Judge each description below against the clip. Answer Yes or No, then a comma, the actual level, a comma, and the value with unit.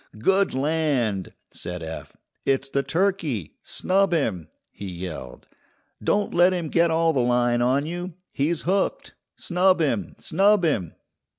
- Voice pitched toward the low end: No, medium, 150 Hz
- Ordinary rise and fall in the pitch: No, wide, 7.4 semitones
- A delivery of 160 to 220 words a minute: No, slow, 135 wpm